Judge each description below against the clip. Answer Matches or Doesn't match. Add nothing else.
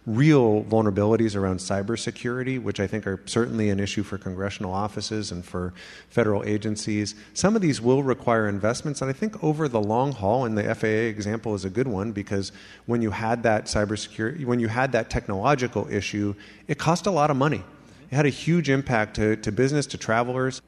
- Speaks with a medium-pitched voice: Doesn't match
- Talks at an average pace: Matches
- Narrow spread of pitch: Doesn't match